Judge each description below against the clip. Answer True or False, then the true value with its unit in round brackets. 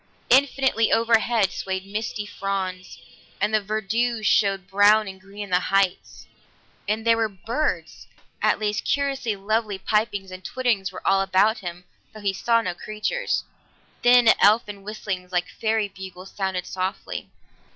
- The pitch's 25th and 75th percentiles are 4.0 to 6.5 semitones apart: False (2.7 semitones)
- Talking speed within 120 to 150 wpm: True (145 wpm)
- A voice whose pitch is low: False (205 Hz)